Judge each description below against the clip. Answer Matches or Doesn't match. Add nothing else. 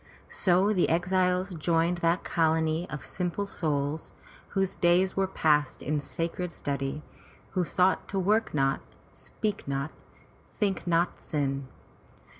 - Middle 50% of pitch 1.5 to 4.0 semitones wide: Matches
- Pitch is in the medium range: Matches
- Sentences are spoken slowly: Matches